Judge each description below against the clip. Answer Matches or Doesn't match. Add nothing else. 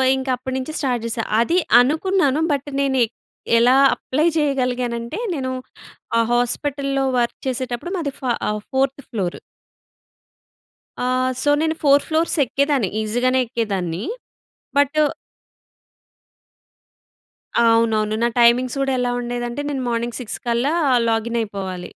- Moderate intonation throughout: Matches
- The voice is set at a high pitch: Matches